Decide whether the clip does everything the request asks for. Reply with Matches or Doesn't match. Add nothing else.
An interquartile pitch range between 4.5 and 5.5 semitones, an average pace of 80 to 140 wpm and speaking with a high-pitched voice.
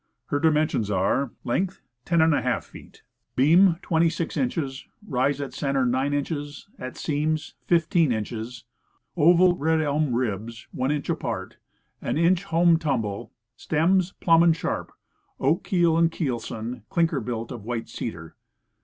Doesn't match